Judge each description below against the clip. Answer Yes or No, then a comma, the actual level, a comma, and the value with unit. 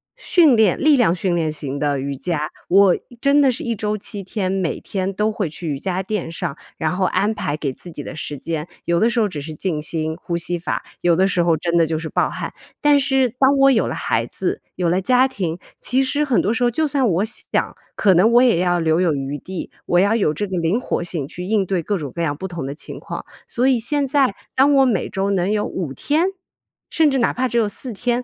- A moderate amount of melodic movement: No, wide, 6.4 semitones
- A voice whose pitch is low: No, high, 190 Hz